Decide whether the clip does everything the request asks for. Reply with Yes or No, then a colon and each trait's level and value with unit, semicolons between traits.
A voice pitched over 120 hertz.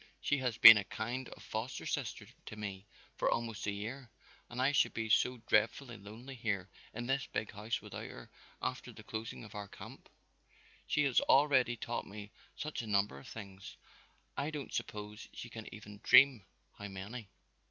No: low, 110 Hz